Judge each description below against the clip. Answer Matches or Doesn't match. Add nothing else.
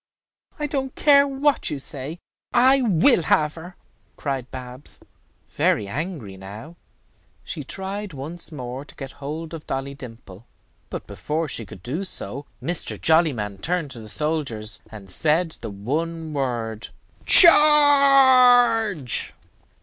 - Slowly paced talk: Matches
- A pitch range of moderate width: Doesn't match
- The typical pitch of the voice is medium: Matches